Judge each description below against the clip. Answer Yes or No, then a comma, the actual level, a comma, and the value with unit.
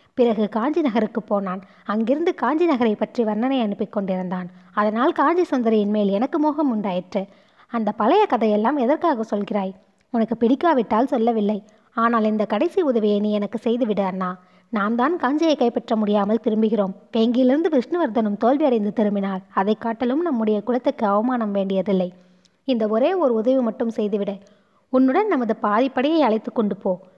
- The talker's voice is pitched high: Yes, high, 225 Hz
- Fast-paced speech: Yes, fast, 135 wpm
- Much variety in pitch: No, average, 3.8 semitones